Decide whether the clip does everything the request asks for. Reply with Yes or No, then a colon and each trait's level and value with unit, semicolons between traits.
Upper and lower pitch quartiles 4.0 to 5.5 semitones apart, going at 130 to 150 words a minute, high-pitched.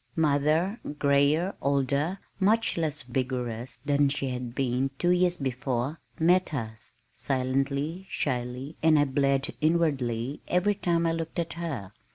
No: average, 4.3 semitones; slow, 135 wpm; medium, 140 Hz